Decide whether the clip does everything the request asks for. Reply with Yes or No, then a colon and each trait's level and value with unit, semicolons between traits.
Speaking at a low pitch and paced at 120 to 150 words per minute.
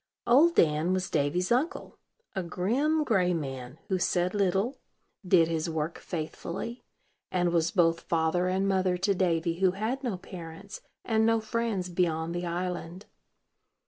No: medium, 180 Hz; average, 145 wpm